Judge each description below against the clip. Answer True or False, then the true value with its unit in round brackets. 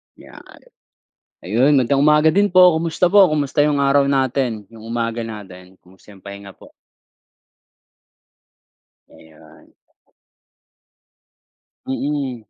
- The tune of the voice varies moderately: False (6.0 semitones)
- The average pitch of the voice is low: True (130 Hz)